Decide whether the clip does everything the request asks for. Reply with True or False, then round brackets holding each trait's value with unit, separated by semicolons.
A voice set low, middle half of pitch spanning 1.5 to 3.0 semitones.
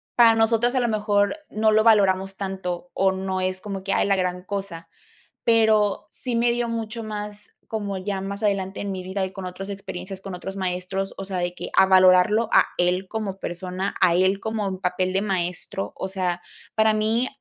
False (195 Hz; 2.4 semitones)